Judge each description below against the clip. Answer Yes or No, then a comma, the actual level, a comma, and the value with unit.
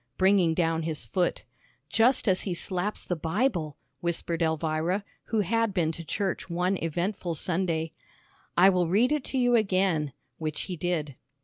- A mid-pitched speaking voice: Yes, medium, 175 Hz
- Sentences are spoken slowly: No, average, 155 wpm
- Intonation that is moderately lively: Yes, average, 3.4 semitones